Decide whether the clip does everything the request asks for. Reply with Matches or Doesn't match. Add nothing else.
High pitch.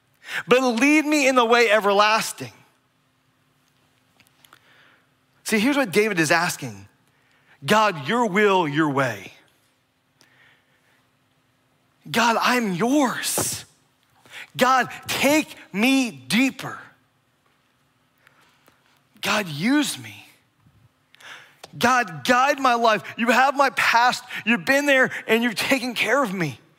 Matches